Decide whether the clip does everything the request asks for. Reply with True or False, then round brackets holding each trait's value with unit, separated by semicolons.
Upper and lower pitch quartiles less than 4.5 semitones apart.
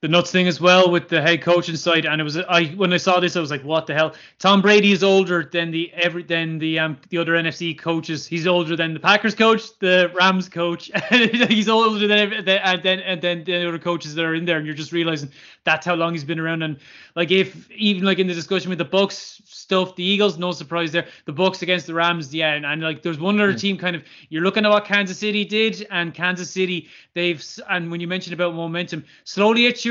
True (2.5 semitones)